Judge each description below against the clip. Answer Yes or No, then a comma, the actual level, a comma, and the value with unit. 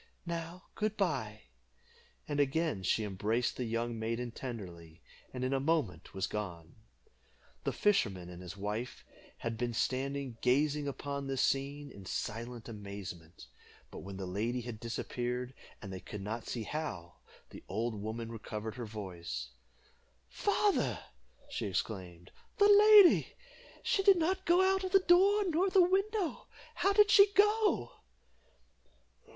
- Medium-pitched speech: No, low, 120 Hz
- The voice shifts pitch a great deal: Yes, wide, 8.6 semitones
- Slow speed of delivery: No, average, 145 wpm